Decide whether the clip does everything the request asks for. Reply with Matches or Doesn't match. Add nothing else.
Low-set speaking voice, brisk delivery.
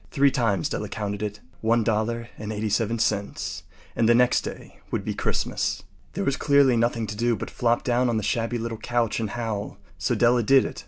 Matches